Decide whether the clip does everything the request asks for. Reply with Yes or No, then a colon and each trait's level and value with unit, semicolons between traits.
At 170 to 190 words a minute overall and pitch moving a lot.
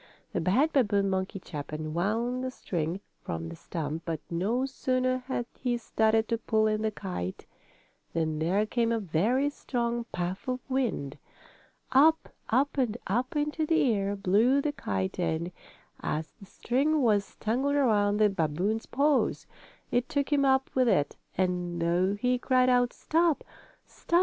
No: average, 160 wpm; wide, 6.2 semitones